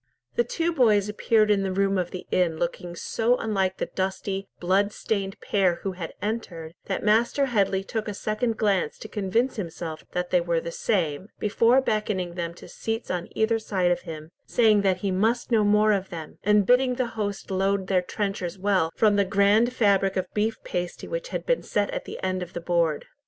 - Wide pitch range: No, average, 3.3 semitones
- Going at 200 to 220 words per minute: Yes, fast, 205 wpm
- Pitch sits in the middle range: No, high, 200 Hz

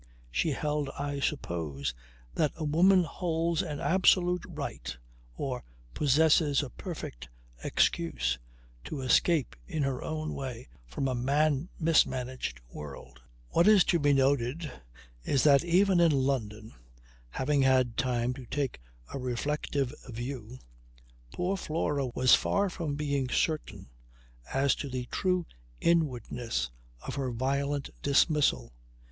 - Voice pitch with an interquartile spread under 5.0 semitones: Yes, average, 4.0 semitones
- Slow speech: Yes, slow, 125 wpm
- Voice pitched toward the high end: No, medium, 140 Hz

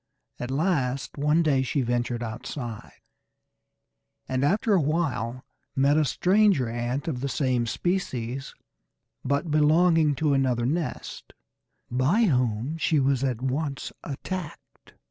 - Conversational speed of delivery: No, slow, 125 wpm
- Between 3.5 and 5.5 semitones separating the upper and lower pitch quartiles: Yes, average, 4.0 semitones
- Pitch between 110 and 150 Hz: Yes, medium, 140 Hz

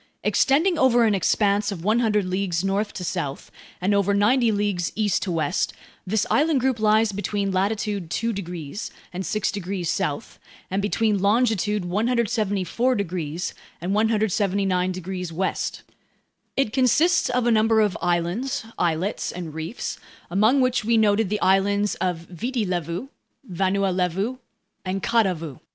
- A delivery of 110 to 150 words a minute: Yes, average, 140 wpm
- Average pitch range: Yes, average, 3.5 semitones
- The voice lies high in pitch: Yes, high, 200 Hz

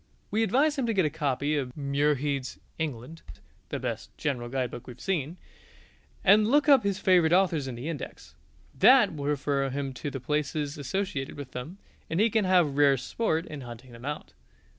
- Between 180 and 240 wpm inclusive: Yes, average, 185 wpm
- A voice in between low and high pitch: Yes, medium, 150 Hz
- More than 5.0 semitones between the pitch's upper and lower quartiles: Yes, wide, 5.5 semitones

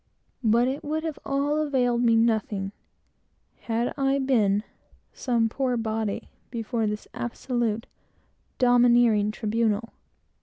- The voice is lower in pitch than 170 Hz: No, high, 235 Hz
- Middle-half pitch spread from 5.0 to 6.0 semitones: No, average, 2.9 semitones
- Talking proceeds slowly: Yes, slow, 110 wpm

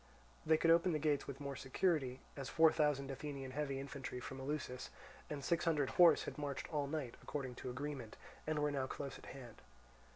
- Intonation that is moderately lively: No, narrow, 2.3 semitones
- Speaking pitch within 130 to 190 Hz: Yes, medium, 140 Hz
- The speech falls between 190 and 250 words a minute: Yes, average, 195 wpm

